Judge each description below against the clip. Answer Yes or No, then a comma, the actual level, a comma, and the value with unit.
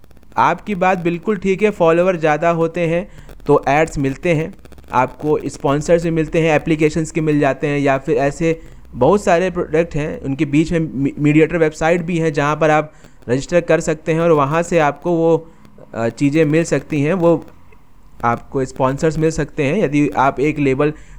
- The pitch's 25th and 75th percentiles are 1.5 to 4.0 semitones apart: Yes, narrow, 2.5 semitones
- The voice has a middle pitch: Yes, medium, 160 Hz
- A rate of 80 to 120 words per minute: No, average, 175 wpm